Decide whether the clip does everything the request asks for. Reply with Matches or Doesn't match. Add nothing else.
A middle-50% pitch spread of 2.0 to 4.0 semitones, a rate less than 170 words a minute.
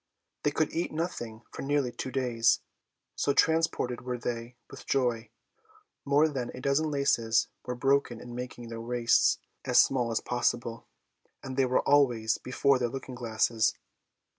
Matches